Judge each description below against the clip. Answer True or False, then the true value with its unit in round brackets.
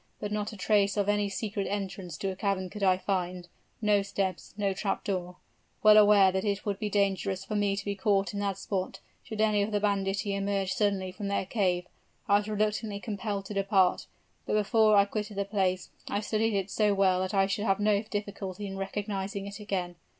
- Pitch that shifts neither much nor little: False (1.3 semitones)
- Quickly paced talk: True (210 wpm)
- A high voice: True (200 Hz)